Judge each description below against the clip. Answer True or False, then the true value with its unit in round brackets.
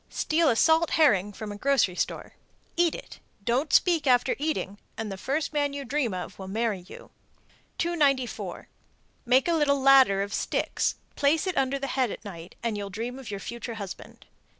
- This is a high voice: True (255 Hz)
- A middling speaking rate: True (185 wpm)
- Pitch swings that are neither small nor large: False (5.9 semitones)